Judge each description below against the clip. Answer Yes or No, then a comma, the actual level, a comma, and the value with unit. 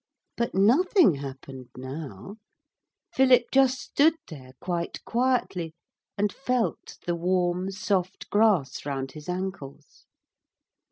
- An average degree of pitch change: No, wide, 8.2 semitones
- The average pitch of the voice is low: No, medium, 185 Hz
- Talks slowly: Yes, slow, 105 wpm